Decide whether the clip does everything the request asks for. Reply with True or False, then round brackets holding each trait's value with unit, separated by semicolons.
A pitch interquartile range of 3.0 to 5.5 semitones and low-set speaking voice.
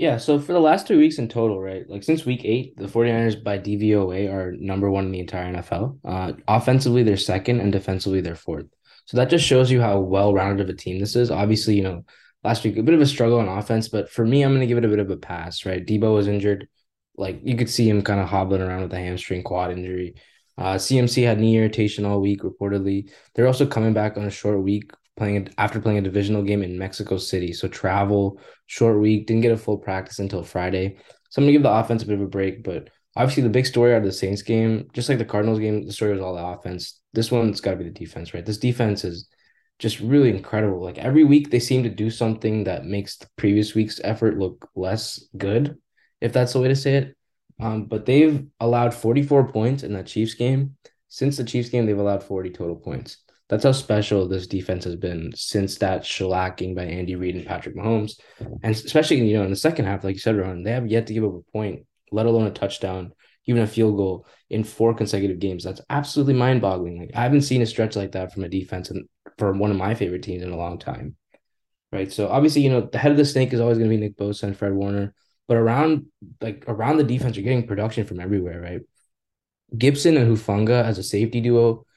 True (3.6 semitones; 105 Hz)